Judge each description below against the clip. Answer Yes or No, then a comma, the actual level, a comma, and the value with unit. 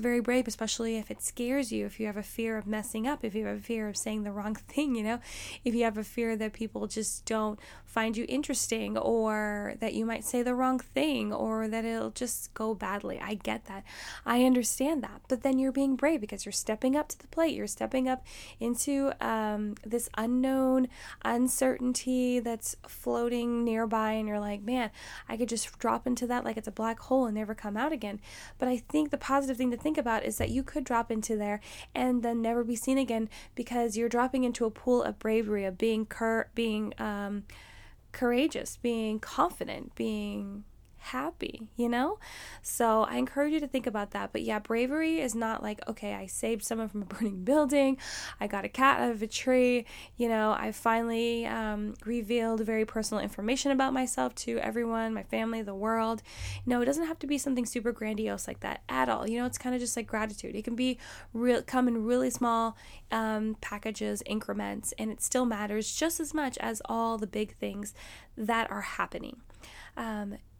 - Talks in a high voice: Yes, high, 230 Hz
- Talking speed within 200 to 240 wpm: Yes, fast, 205 wpm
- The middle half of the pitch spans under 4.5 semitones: Yes, average, 2.7 semitones